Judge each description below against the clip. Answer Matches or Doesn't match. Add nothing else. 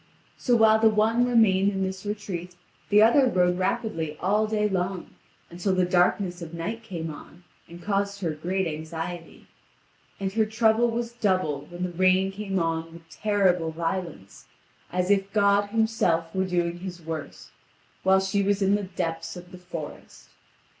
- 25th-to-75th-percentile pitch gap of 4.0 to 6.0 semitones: Doesn't match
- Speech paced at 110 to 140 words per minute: Doesn't match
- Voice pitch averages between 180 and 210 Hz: Matches